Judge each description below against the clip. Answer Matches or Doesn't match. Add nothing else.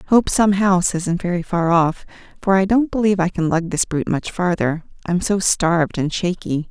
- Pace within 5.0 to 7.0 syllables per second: Matches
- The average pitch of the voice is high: Doesn't match